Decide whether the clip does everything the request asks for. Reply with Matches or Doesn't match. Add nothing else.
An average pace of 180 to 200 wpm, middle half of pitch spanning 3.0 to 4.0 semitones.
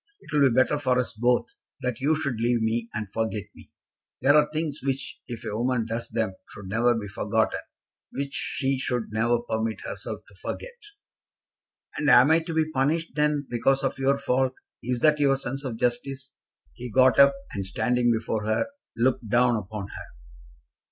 Matches